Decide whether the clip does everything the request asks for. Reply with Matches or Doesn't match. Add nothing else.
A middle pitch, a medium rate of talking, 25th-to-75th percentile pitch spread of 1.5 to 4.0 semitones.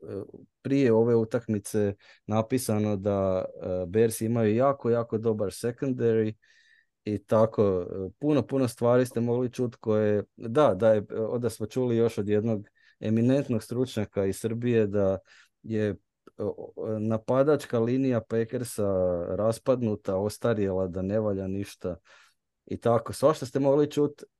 Doesn't match